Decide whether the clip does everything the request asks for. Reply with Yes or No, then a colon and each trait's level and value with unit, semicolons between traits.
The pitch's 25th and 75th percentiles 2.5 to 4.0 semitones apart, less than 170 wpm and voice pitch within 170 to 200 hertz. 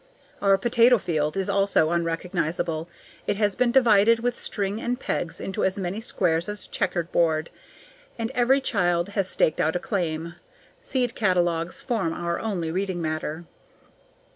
No: average, 4.7 semitones; average, 155 wpm; high, 190 Hz